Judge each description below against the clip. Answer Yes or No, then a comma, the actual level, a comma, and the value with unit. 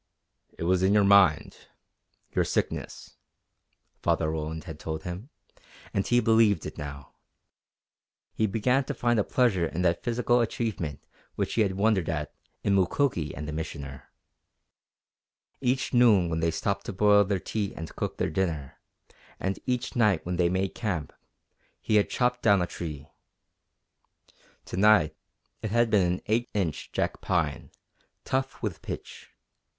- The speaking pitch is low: Yes, very low, 95 Hz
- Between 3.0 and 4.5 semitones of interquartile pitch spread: No, average, 5.3 semitones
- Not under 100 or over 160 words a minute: Yes, average, 155 wpm